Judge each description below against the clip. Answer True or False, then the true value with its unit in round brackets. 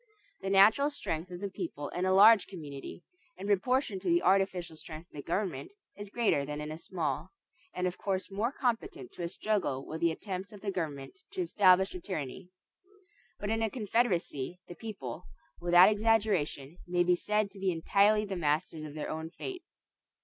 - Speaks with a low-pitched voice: False (185 Hz)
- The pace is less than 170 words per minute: False (185 wpm)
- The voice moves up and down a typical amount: True (4.4 semitones)